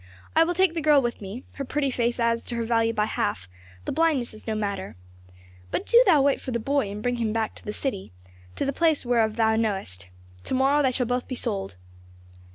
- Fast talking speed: Yes, fast, 225 wpm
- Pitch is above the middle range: Yes, high, 240 Hz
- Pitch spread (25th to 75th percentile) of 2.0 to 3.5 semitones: No, average, 4.3 semitones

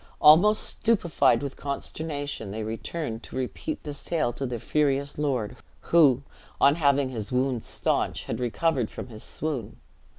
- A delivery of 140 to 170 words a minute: Yes, average, 145 wpm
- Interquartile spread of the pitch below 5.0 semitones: Yes, average, 4.0 semitones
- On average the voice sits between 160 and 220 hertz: No, medium, 140 Hz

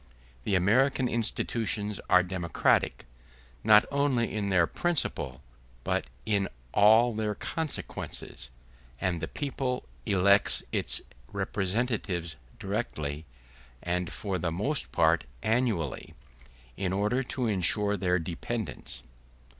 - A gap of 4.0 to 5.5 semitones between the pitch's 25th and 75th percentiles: Yes, average, 4.7 semitones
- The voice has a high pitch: No, low, 100 Hz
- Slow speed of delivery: Yes, slow, 105 wpm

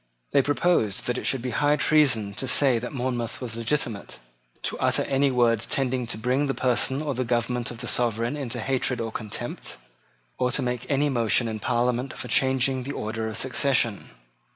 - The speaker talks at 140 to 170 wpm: No, average, 185 wpm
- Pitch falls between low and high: No, low, 125 Hz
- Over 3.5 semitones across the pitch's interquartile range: No, narrow, 2.5 semitones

